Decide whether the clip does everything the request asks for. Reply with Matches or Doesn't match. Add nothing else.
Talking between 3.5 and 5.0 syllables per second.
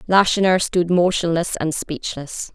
Matches